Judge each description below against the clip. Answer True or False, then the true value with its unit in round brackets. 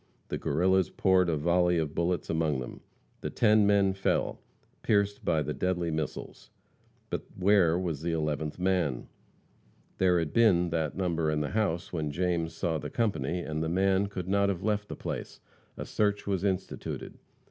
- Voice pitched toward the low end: True (90 Hz)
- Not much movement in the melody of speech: False (3.3 semitones)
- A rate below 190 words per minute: True (170 wpm)